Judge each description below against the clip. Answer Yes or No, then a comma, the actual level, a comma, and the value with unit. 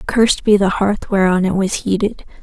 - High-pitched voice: Yes, high, 200 Hz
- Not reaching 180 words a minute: No, average, 200 wpm